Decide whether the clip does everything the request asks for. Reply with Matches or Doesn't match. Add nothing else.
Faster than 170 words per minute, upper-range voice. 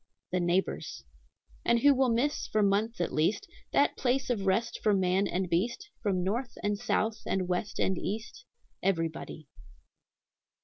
Doesn't match